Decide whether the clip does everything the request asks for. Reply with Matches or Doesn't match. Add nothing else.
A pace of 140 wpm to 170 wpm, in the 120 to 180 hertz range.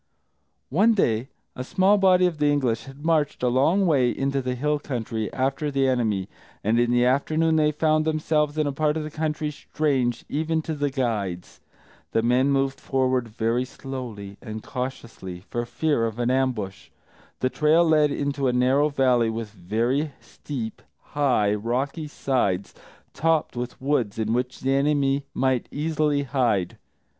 Matches